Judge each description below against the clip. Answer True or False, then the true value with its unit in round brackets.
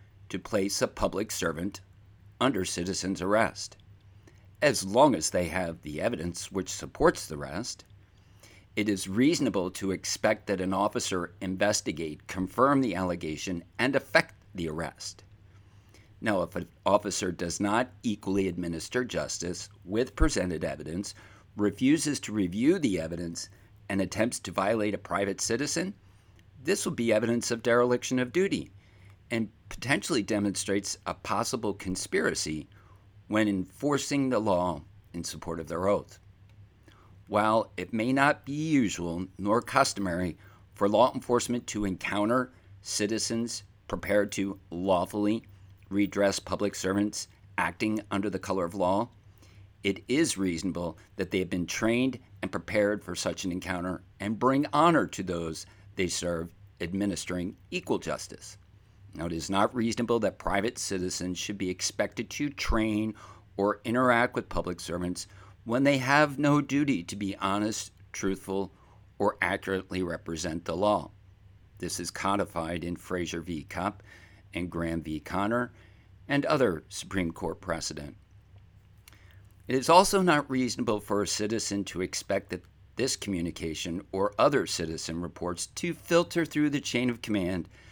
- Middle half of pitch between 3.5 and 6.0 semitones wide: False (2.7 semitones)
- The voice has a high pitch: False (100 Hz)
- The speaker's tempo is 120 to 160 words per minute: True (140 wpm)